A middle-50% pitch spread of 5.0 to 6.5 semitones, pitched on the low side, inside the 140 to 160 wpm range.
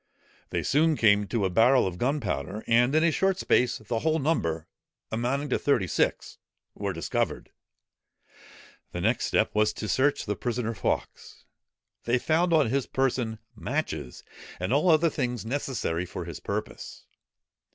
Yes: average, 5.3 semitones; low, 120 Hz; average, 150 wpm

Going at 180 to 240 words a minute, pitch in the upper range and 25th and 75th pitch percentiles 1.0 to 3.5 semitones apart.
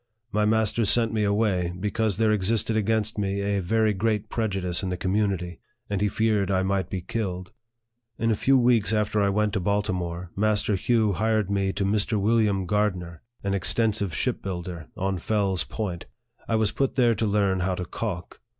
No: average, 185 wpm; low, 100 Hz; narrow, 2.6 semitones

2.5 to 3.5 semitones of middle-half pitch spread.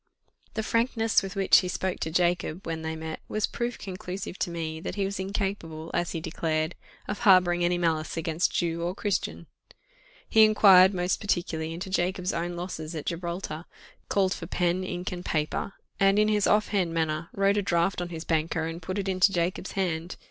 Yes: average, 2.9 semitones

